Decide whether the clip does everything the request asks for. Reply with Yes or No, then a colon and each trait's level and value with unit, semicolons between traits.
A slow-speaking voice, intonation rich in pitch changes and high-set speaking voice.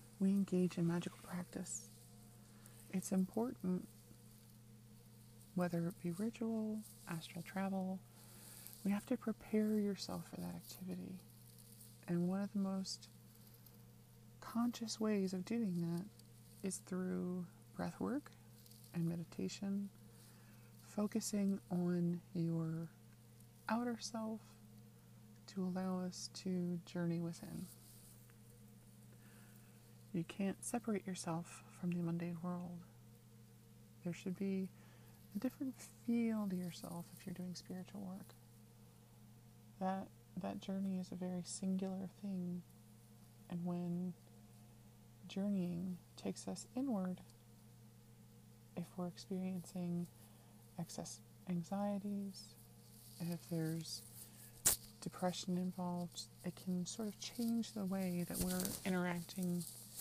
No: slow, 100 wpm; wide, 8.6 semitones; medium, 170 Hz